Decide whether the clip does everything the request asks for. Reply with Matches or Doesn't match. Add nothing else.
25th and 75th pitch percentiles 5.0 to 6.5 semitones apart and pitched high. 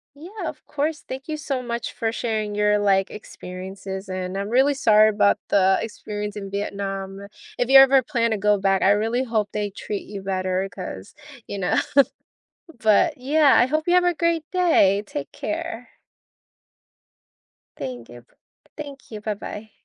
Matches